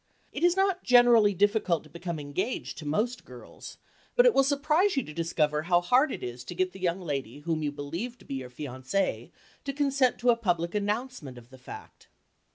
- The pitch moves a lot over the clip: Yes, wide, 8.8 semitones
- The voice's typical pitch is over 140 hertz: Yes, medium, 185 Hz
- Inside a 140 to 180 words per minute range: No, fast, 205 wpm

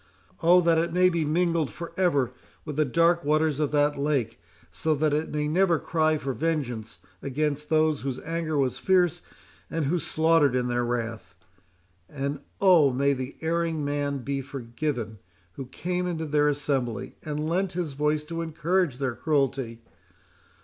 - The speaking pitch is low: No, medium, 150 Hz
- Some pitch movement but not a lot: Yes, average, 3.6 semitones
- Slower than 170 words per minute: Yes, average, 160 wpm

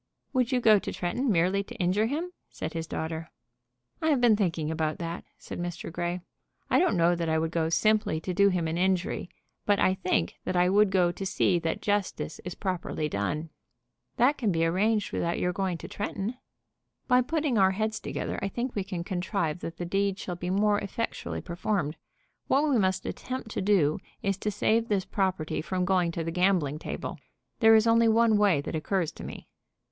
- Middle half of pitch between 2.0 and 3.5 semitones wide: No, average, 4.0 semitones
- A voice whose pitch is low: No, high, 190 Hz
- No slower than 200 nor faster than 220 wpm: Yes, fast, 205 wpm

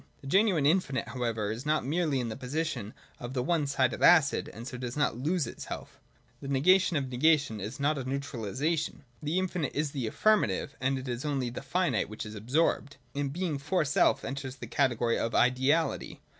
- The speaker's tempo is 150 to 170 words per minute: No, average, 190 wpm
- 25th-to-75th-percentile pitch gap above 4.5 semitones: No, average, 3.8 semitones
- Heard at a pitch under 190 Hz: Yes, medium, 140 Hz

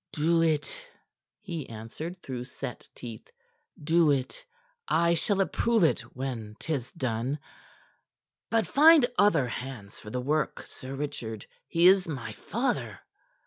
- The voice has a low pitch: No, medium, 145 Hz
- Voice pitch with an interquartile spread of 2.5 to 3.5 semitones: No, wide, 5.6 semitones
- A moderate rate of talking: No, slow, 130 wpm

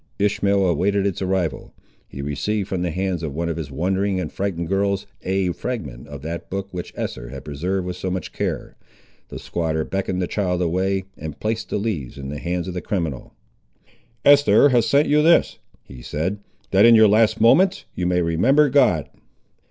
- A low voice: Yes, very low, 95 Hz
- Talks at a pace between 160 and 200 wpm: Yes, average, 190 wpm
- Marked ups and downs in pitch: No, average, 3.7 semitones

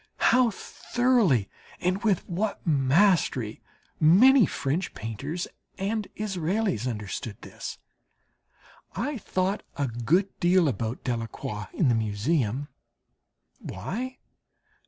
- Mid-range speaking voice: Yes, medium, 170 Hz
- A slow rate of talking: Yes, slow, 95 wpm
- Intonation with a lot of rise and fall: Yes, wide, 9.0 semitones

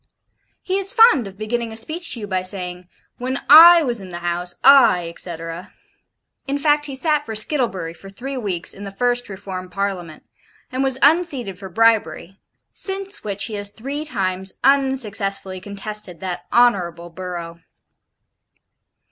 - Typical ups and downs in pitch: No, wide, 6.5 semitones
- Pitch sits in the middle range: No, high, 205 Hz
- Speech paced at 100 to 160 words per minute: Yes, average, 155 wpm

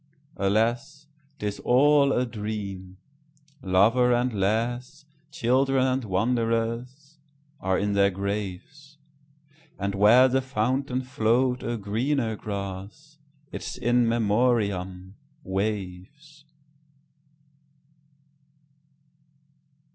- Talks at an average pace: No, slow, 70 wpm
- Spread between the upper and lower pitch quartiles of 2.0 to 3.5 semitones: No, wide, 5.5 semitones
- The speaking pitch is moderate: No, low, 120 Hz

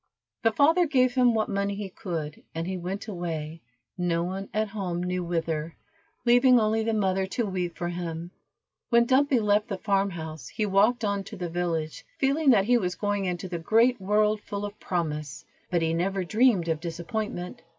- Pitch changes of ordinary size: Yes, average, 4.1 semitones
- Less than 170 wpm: No, average, 190 wpm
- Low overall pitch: No, high, 195 Hz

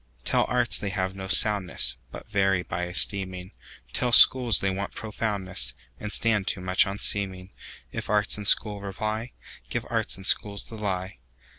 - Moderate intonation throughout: No, narrow, 2.3 semitones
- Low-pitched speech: Yes, low, 100 Hz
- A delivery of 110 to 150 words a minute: Yes, average, 140 wpm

